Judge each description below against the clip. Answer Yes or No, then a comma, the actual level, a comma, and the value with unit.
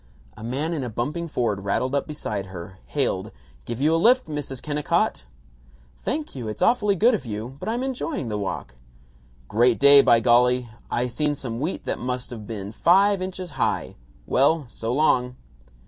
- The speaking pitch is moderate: No, low, 130 Hz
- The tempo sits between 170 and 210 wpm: Yes, average, 180 wpm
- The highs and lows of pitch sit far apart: Yes, wide, 5.9 semitones